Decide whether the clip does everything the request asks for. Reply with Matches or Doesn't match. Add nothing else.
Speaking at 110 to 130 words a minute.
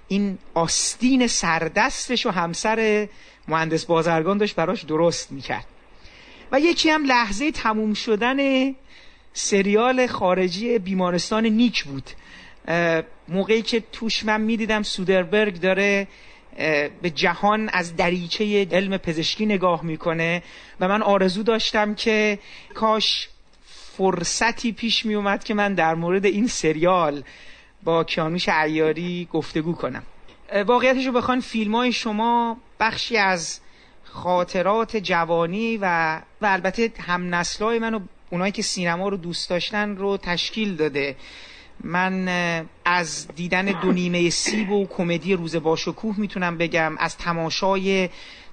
Matches